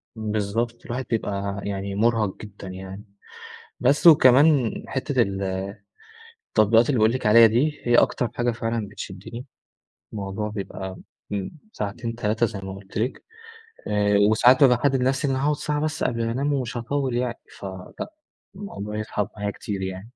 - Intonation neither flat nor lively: Yes, average, 3.7 semitones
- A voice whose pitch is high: No, low, 115 Hz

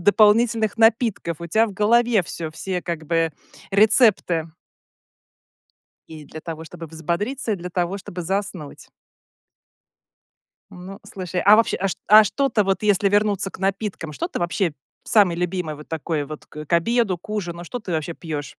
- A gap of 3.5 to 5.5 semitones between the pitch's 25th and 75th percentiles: Yes, average, 4.1 semitones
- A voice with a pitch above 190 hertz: No, medium, 185 Hz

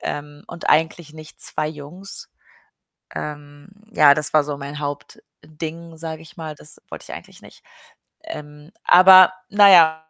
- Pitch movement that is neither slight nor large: No, narrow, 2.2 semitones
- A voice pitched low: No, medium, 155 Hz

